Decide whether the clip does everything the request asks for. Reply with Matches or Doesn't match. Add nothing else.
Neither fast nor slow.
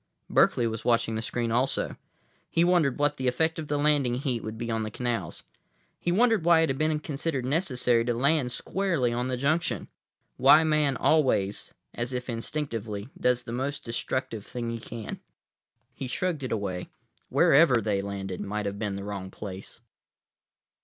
Matches